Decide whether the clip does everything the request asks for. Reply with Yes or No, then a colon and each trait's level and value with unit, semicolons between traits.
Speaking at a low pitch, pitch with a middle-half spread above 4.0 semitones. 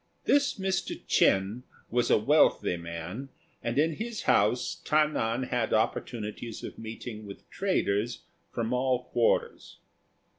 Yes: low, 120 Hz; average, 4.9 semitones